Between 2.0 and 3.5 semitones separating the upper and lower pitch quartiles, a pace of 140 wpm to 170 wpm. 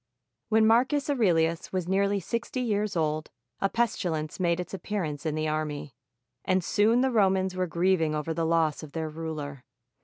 No: average, 4.7 semitones; average, 165 wpm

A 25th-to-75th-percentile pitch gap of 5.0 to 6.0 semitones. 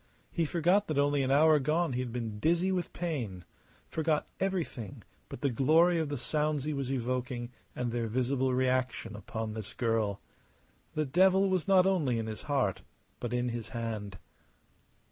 Yes: average, 5.3 semitones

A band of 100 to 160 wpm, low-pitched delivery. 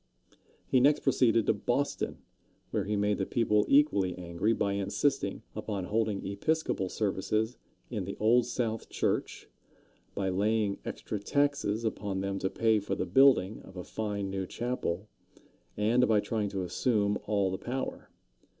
Yes: average, 150 wpm; low, 105 Hz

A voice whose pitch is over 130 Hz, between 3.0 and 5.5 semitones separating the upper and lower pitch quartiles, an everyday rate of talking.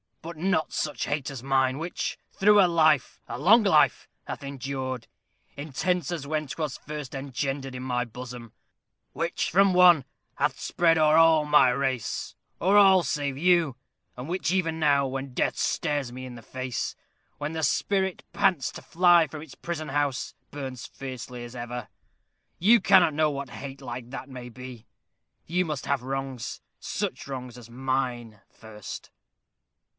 Yes: medium, 140 Hz; average, 4.2 semitones; average, 160 wpm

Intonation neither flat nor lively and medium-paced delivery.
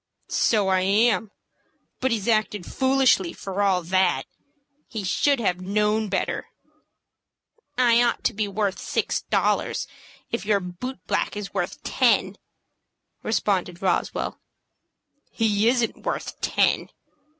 No: average, 3.4 semitones; slow, 120 wpm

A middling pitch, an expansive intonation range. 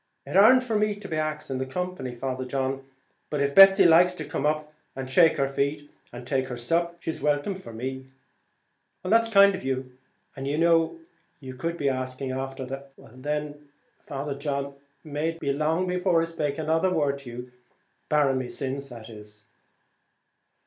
No: medium, 145 Hz; average, 3.9 semitones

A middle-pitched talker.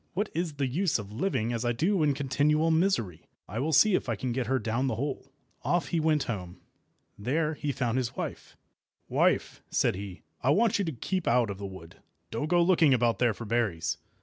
No: low, 130 Hz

